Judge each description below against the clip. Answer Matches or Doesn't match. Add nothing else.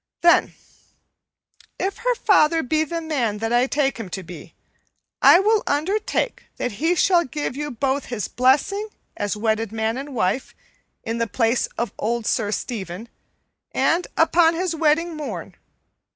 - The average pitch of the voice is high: Matches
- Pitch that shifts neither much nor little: Doesn't match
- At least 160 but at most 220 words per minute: Doesn't match